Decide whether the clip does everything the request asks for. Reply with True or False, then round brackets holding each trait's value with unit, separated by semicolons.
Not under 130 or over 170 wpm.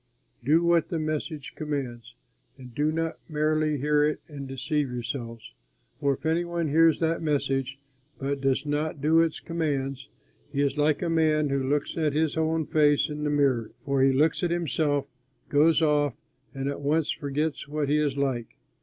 False (180 wpm)